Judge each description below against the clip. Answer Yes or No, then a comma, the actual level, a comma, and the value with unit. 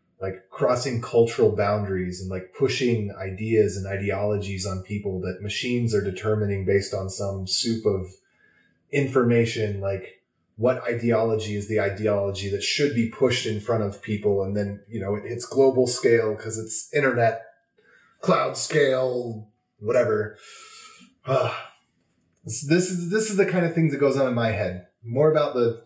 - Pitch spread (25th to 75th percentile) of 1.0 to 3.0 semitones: No, average, 3.8 semitones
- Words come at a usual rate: Yes, average, 160 wpm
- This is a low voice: Yes, low, 110 Hz